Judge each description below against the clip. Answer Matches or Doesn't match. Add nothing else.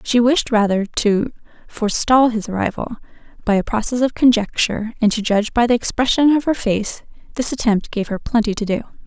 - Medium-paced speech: Matches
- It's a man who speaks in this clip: Doesn't match